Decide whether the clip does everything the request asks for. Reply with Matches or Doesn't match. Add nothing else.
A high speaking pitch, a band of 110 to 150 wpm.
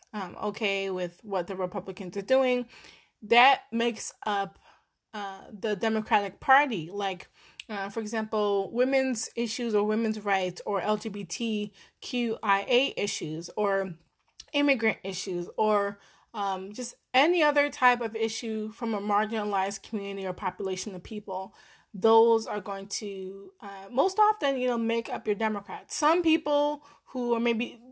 Matches